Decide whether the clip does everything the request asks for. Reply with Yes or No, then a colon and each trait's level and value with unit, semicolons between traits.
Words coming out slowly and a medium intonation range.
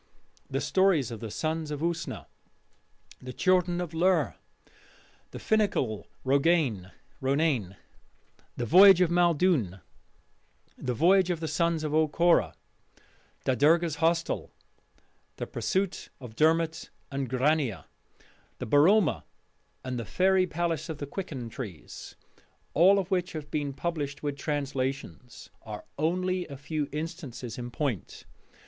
Yes: slow, 125 wpm; average, 4.8 semitones